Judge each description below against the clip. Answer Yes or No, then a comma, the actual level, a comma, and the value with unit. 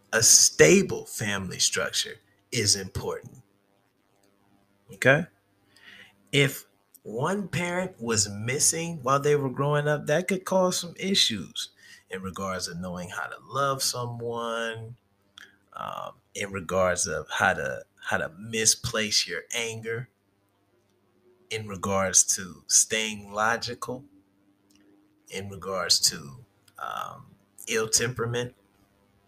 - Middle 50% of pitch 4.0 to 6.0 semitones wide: Yes, average, 4.5 semitones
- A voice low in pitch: Yes, low, 110 Hz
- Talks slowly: Yes, slow, 105 wpm